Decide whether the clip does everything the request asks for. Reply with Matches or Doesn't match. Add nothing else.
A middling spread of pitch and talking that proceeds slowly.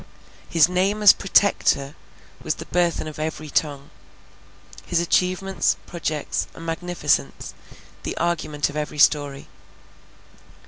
Matches